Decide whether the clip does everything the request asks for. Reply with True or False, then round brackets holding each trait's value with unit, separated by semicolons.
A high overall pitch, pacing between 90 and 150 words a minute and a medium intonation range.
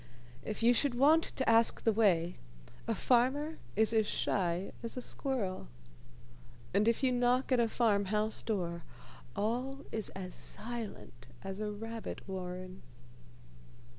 True (220 Hz; 140 wpm; 4.1 semitones)